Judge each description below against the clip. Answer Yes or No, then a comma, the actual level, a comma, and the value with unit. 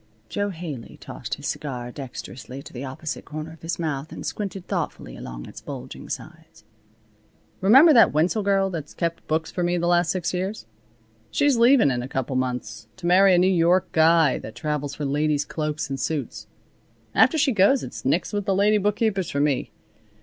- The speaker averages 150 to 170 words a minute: No, average, 195 wpm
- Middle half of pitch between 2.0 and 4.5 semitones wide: No, wide, 5.5 semitones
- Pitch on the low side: No, medium, 165 Hz